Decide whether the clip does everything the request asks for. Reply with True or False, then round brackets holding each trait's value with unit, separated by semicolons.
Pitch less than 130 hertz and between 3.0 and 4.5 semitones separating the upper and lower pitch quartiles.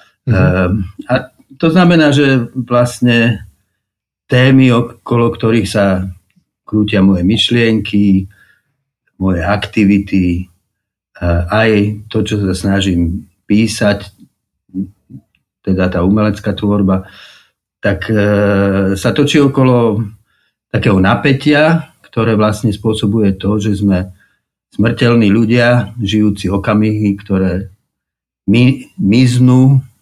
True (105 Hz; 3.4 semitones)